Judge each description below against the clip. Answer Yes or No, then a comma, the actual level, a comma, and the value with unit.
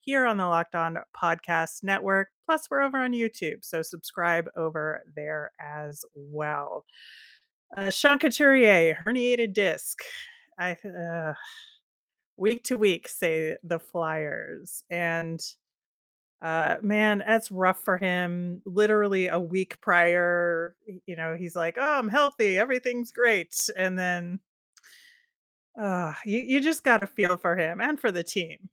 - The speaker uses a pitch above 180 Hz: Yes, high, 190 Hz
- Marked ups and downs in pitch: Yes, wide, 5.8 semitones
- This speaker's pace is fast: No, average, 140 wpm